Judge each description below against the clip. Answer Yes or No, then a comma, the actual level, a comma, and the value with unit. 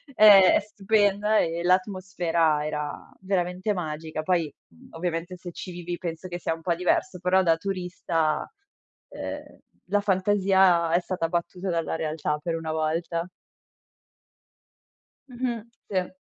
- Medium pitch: Yes, medium, 175 Hz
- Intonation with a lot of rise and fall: No, narrow, 2.5 semitones